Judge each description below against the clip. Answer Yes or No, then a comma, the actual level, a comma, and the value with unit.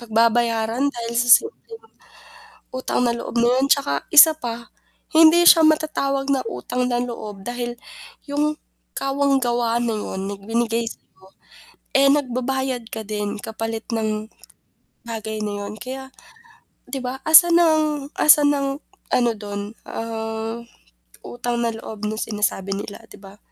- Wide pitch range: No, average, 3.6 semitones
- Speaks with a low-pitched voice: No, high, 235 Hz